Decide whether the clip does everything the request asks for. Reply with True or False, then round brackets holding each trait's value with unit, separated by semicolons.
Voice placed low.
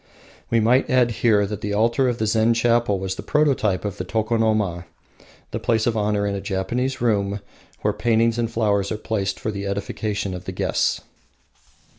True (110 Hz)